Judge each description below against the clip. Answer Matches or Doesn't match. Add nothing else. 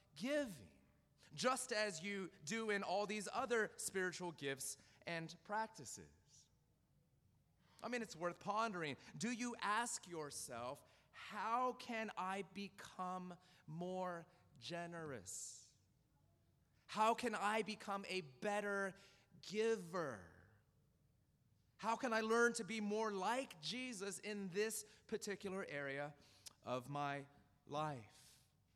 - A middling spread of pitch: Doesn't match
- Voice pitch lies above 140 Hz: Matches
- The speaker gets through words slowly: Matches